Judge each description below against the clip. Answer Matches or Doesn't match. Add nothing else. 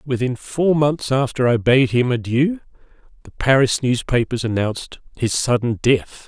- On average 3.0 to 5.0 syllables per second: Matches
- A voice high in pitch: Doesn't match